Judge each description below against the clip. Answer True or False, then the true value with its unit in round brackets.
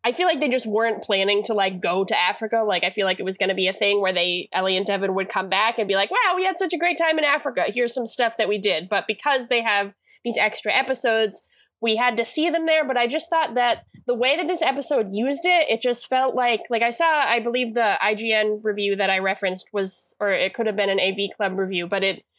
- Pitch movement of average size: True (4.6 semitones)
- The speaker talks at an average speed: False (270 wpm)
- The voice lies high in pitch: True (225 Hz)